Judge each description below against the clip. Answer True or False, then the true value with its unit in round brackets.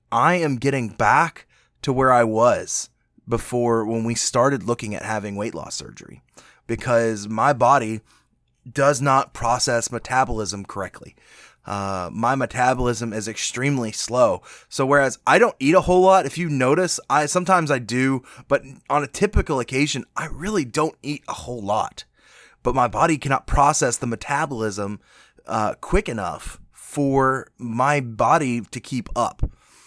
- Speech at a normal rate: True (150 wpm)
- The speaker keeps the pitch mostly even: False (3.7 semitones)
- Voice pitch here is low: True (125 Hz)